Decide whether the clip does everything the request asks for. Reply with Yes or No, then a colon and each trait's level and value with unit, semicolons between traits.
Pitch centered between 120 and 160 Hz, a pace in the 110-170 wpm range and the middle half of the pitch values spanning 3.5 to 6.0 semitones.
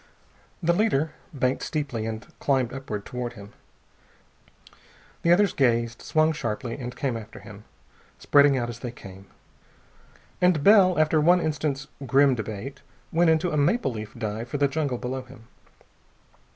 Yes: low, 135 Hz; average, 150 wpm; average, 4.9 semitones